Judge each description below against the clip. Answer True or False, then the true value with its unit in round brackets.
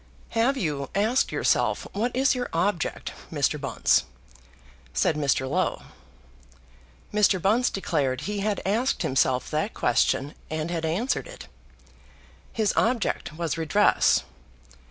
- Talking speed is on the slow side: True (120 wpm)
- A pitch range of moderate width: False (6.5 semitones)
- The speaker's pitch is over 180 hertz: True (190 Hz)